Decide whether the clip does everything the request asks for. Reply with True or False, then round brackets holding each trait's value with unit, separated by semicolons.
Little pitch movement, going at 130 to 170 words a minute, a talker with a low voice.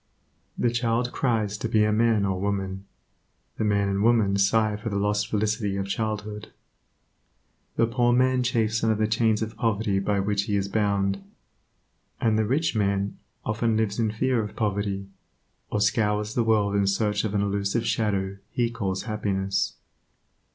True (2.0 semitones; 165 wpm; 105 Hz)